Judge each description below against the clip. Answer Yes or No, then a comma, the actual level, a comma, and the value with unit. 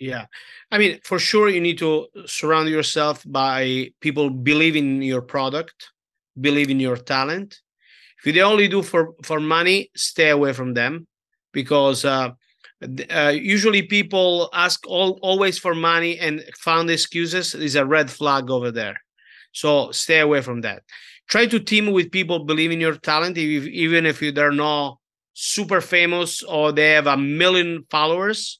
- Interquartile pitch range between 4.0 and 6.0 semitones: No, average, 3.6 semitones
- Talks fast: No, average, 160 wpm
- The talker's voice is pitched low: No, medium, 155 Hz